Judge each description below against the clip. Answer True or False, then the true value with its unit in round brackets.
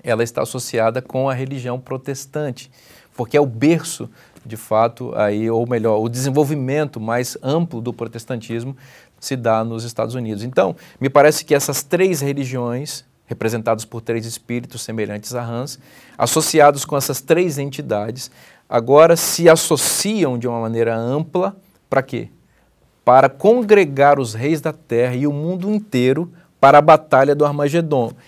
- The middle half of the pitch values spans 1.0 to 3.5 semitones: False (4.3 semitones)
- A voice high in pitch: False (130 Hz)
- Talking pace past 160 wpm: False (150 wpm)